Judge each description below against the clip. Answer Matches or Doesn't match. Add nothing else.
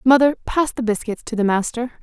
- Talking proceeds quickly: Matches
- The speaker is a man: Doesn't match